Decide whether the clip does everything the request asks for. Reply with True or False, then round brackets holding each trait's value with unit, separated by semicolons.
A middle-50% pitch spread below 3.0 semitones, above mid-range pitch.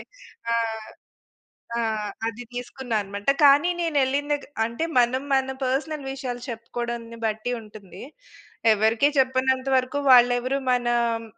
True (2.5 semitones; 245 Hz)